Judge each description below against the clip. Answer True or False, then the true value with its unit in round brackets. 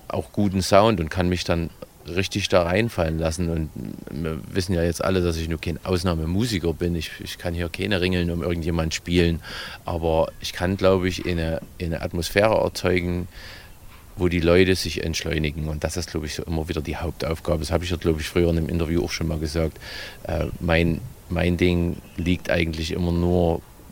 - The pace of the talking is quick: True (195 wpm)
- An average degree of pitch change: False (1.9 semitones)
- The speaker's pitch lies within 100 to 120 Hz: False (85 Hz)